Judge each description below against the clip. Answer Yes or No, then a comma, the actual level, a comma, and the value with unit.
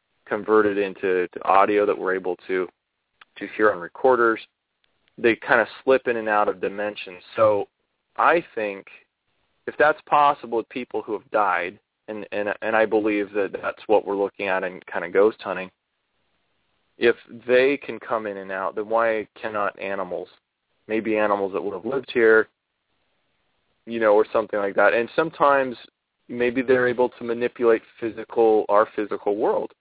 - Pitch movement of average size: Yes, average, 3.3 semitones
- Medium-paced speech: Yes, average, 165 wpm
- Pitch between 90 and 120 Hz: Yes, low, 110 Hz